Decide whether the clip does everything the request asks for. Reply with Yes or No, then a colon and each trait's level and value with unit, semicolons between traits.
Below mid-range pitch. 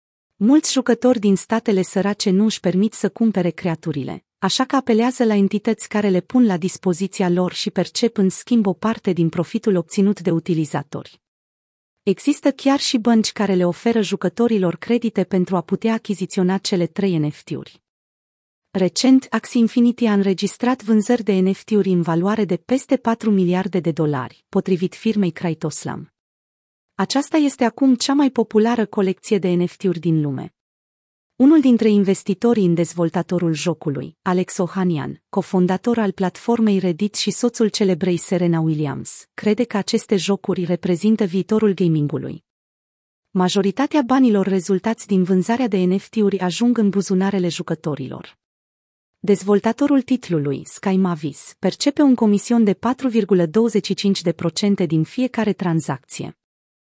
No: high, 195 Hz